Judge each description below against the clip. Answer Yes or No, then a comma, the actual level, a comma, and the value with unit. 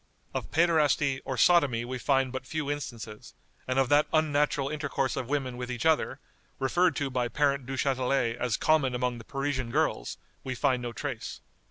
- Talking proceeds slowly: No, average, 175 wpm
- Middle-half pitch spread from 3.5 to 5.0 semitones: No, narrow, 2.6 semitones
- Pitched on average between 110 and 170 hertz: Yes, low, 135 Hz